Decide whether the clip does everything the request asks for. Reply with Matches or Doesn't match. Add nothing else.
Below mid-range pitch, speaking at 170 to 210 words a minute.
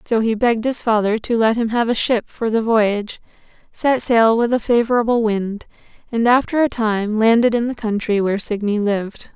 Doesn't match